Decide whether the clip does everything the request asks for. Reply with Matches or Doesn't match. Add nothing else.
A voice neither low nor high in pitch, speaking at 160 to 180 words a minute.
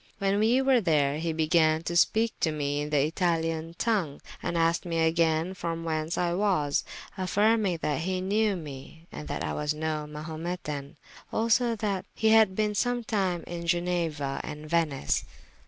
Matches